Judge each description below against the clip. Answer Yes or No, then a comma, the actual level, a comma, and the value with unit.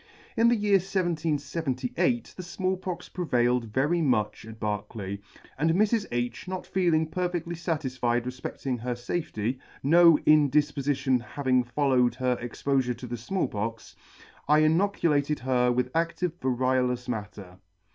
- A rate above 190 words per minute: No, slow, 135 wpm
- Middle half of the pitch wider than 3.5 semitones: Yes, wide, 5.5 semitones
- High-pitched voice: No, low, 135 Hz